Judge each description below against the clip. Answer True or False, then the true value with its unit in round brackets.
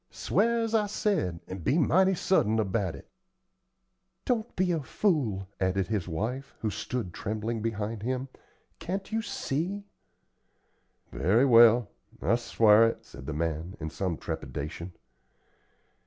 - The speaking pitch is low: True (115 Hz)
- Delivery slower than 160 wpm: True (135 wpm)